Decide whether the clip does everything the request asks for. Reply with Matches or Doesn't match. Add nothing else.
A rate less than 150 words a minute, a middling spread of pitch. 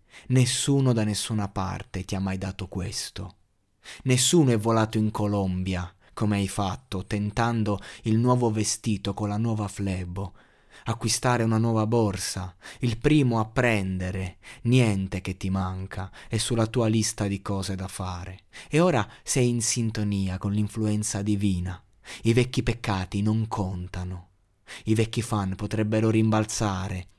Matches